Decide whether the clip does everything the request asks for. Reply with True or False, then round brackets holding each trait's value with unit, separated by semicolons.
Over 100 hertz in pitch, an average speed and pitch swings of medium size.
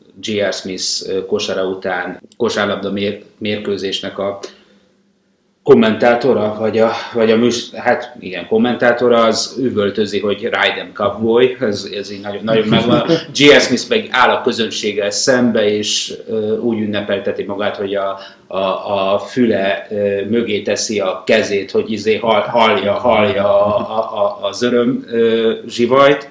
True (110 Hz; 130 wpm; 3.1 semitones)